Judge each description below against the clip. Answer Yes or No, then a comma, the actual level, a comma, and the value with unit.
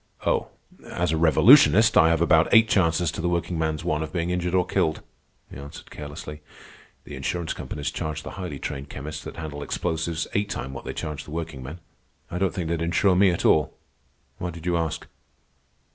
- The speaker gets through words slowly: No, average, 190 wpm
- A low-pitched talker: Yes, very low, 80 Hz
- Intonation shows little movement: Yes, narrow, 2.3 semitones